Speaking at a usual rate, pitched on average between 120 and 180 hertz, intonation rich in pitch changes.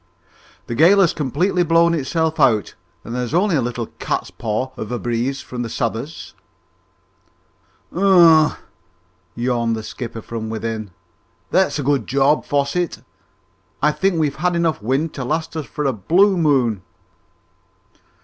Yes: average, 145 wpm; medium, 140 Hz; wide, 5.7 semitones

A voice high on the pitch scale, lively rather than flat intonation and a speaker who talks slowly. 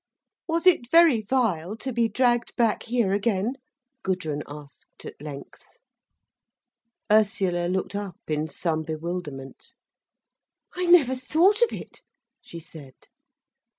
Yes: high, 200 Hz; wide, 7.7 semitones; slow, 120 wpm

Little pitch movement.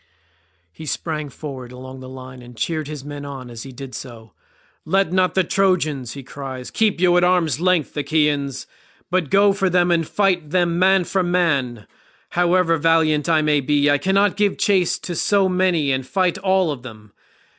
No: average, 5.2 semitones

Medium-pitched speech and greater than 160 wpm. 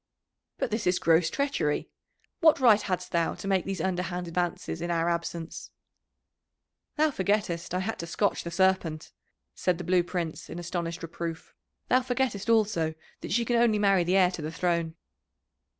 Yes: medium, 180 Hz; average, 170 wpm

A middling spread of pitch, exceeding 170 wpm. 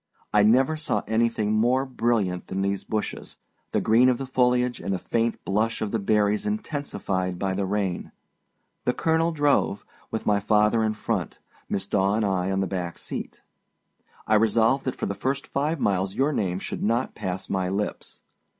Yes: average, 4.2 semitones; average, 180 wpm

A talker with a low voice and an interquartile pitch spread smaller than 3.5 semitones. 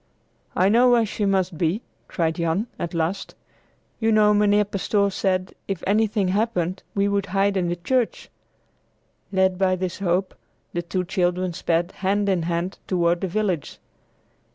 No: high, 190 Hz; average, 2.7 semitones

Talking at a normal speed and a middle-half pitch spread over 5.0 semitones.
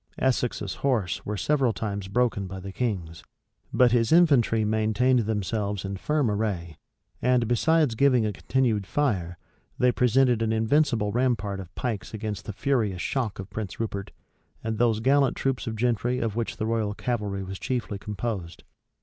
No: average, 160 wpm; average, 3.7 semitones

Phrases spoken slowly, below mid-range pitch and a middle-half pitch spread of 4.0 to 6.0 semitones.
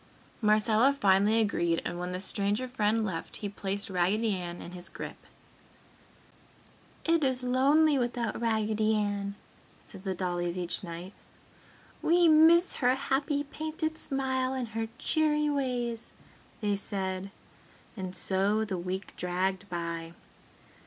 No: slow, 130 wpm; high, 215 Hz; wide, 5.6 semitones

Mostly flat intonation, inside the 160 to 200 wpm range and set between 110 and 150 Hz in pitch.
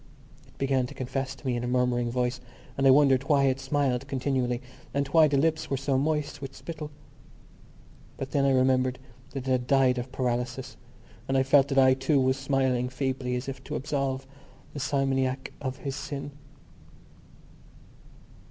Yes: narrow, 1.3 semitones; average, 175 wpm; low, 135 Hz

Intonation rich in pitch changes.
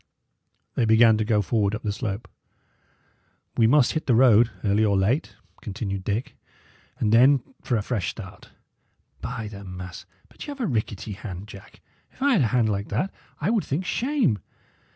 No: average, 4.2 semitones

